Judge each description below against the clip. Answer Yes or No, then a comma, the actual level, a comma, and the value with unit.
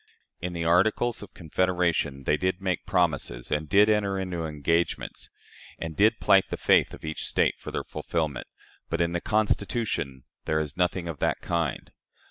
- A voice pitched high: No, very low, 85 Hz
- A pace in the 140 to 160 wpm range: No, average, 170 wpm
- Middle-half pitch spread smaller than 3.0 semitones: No, average, 3.5 semitones